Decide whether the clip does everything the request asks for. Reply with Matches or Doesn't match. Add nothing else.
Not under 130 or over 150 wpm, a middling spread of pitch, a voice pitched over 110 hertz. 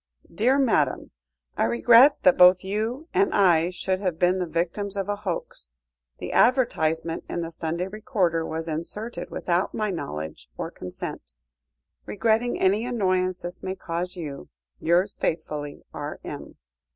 Matches